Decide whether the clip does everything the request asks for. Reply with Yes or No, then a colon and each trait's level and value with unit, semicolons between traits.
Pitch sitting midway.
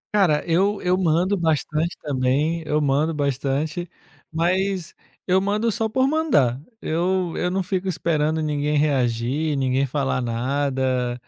Yes: medium, 155 Hz